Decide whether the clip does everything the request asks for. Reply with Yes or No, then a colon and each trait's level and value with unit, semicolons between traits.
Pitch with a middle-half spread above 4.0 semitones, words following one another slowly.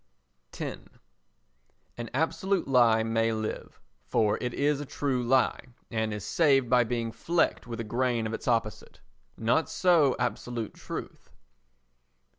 No: average, 3.3 semitones; slow, 130 wpm